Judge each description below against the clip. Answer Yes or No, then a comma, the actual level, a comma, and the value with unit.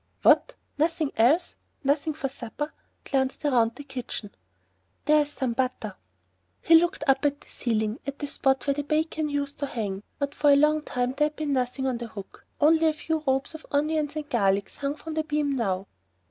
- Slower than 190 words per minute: No, average, 200 wpm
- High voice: Yes, very high, 285 Hz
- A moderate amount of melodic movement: Yes, average, 3.4 semitones